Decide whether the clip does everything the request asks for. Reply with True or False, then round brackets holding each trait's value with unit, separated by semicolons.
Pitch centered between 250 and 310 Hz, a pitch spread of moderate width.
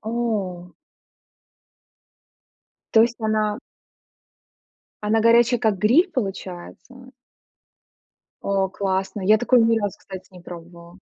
False (210 Hz; 3.5 semitones)